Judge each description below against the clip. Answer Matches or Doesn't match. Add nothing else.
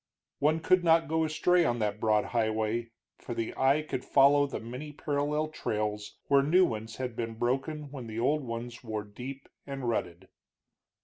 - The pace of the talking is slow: Doesn't match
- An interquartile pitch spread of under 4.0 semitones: Doesn't match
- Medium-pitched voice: Doesn't match